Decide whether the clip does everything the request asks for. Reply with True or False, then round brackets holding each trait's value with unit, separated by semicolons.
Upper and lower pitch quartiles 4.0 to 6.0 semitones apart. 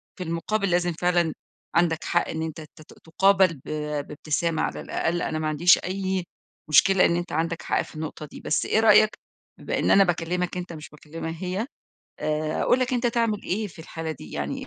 False (3.1 semitones)